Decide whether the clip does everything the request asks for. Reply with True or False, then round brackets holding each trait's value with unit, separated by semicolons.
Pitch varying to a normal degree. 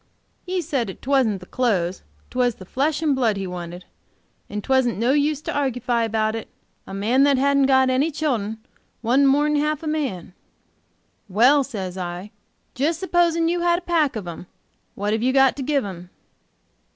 False (5.8 semitones)